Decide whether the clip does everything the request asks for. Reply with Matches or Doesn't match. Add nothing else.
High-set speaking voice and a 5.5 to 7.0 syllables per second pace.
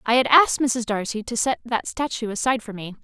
Matches